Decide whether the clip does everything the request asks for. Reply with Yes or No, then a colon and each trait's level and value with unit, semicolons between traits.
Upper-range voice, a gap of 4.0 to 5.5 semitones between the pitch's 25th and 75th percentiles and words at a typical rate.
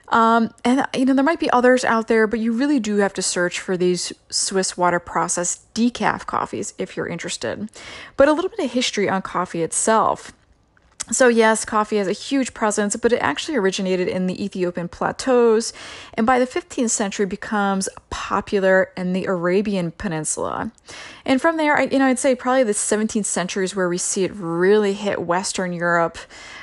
Yes: high, 210 Hz; average, 4.9 semitones; average, 185 wpm